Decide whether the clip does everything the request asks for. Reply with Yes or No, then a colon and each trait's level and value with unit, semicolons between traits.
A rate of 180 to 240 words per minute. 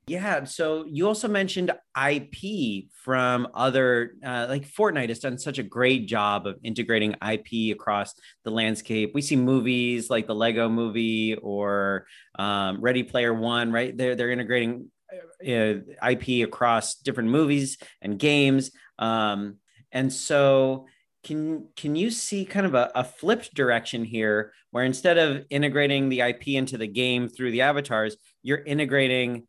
No: average, 155 wpm